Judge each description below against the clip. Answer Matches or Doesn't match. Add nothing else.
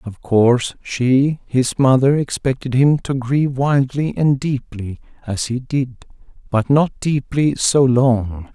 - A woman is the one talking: Doesn't match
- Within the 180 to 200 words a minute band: Doesn't match